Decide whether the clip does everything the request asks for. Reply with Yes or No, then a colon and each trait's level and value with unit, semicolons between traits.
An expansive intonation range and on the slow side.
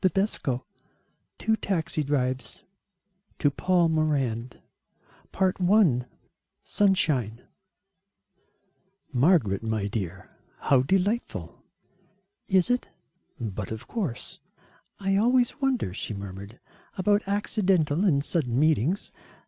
Yes: wide, 8.4 semitones; slow, 90 wpm